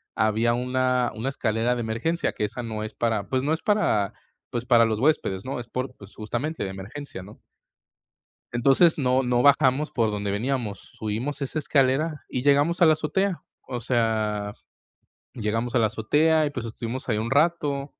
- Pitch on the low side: Yes, low, 125 Hz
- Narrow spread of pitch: No, average, 4.4 semitones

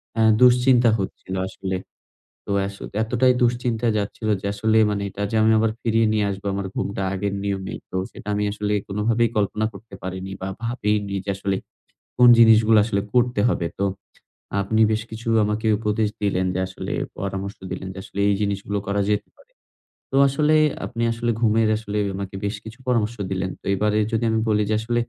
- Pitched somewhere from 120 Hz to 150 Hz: No, low, 105 Hz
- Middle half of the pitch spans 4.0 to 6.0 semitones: No, narrow, 2.5 semitones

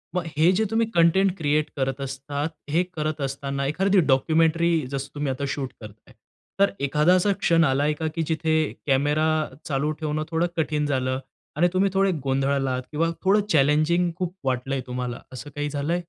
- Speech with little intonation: No, average, 3.6 semitones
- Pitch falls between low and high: Yes, medium, 150 Hz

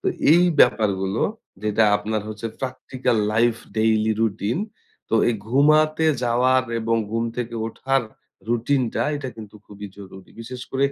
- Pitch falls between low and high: No, low, 115 Hz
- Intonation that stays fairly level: No, average, 3.2 semitones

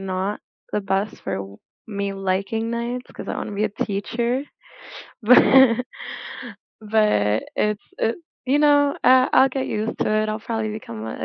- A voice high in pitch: Yes, high, 215 Hz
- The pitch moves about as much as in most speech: Yes, average, 3.6 semitones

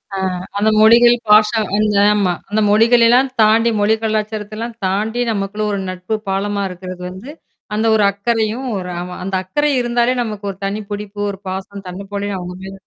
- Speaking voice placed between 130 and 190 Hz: No, high, 210 Hz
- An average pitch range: No, narrow, 2.3 semitones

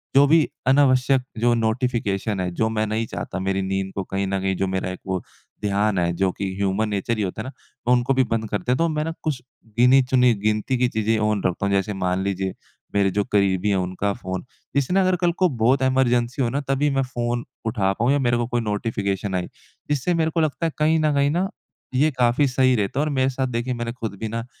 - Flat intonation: No, average, 5.0 semitones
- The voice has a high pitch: No, low, 115 Hz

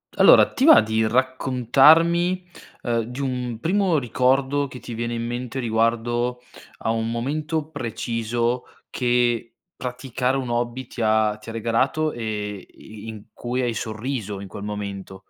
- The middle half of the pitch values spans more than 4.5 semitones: No, average, 2.7 semitones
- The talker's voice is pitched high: No, low, 120 Hz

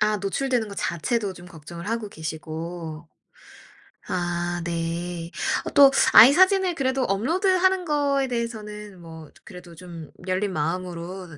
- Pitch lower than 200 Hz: Yes, medium, 185 Hz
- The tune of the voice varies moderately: No, wide, 6.3 semitones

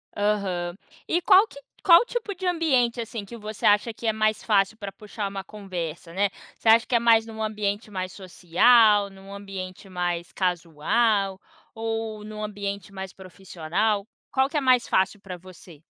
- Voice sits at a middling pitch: No, high, 205 Hz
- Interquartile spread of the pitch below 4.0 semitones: Yes, average, 3.0 semitones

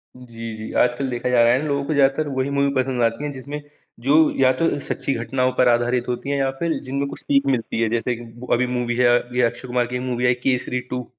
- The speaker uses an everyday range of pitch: No, narrow, 2.2 semitones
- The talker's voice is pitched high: No, low, 125 Hz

